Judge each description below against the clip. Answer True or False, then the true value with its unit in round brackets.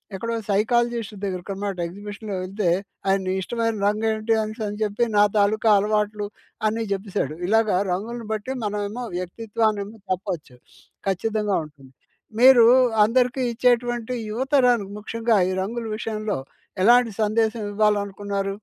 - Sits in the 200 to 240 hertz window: True (215 Hz)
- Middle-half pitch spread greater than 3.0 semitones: False (2.4 semitones)